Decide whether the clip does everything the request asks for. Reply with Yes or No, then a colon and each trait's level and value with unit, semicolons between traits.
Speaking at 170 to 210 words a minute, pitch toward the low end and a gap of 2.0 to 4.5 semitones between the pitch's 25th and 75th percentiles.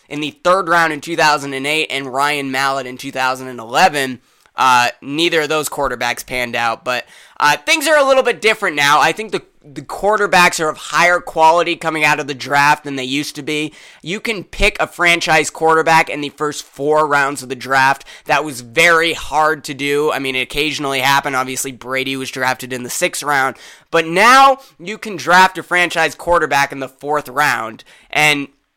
No: average, 190 wpm; medium, 150 Hz; average, 3.5 semitones